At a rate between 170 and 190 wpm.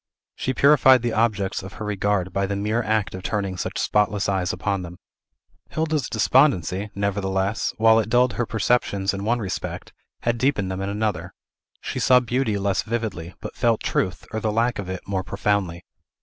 Yes: average, 180 wpm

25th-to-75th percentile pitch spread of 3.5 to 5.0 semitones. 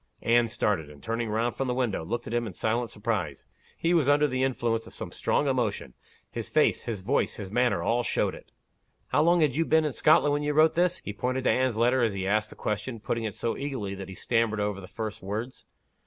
Yes: average, 4.0 semitones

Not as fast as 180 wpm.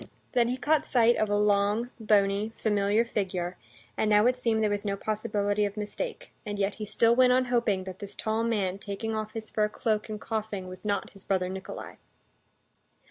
No: average, 195 wpm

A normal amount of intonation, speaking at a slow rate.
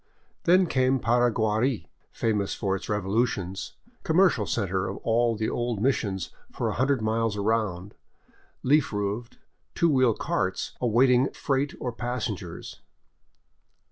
Yes: average, 3.9 semitones; slow, 120 wpm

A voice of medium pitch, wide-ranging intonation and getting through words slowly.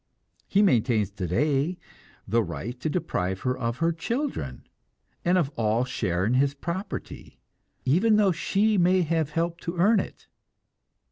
No: medium, 150 Hz; wide, 7.6 semitones; average, 145 wpm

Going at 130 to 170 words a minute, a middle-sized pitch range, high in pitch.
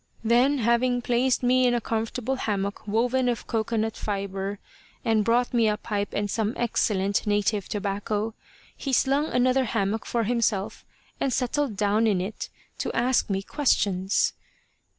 Yes: average, 150 wpm; average, 3.1 semitones; high, 225 Hz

